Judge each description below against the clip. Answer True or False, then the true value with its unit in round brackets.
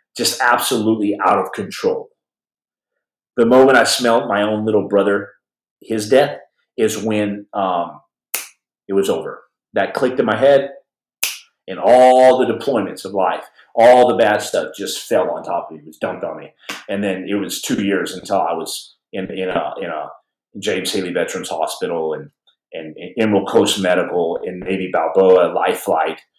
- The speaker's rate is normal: True (170 wpm)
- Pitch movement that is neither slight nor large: True (4.2 semitones)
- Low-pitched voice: True (105 Hz)